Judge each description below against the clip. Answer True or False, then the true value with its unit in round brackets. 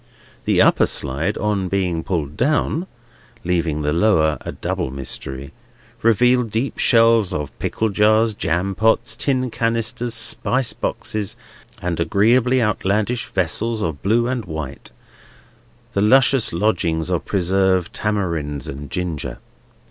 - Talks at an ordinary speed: False (125 wpm)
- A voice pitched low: True (100 Hz)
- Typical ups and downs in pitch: False (5.7 semitones)